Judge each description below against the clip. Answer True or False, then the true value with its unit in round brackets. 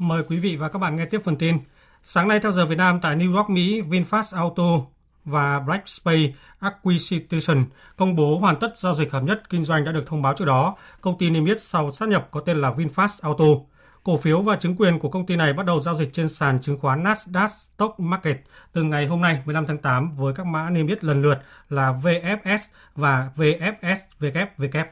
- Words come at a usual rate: True (220 wpm)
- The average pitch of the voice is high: False (165 Hz)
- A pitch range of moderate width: True (3.8 semitones)